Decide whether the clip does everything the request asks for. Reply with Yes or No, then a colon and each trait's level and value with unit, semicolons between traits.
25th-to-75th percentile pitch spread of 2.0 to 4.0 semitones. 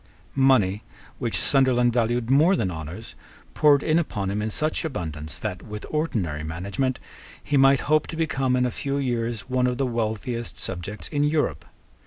No: wide, 5.5 semitones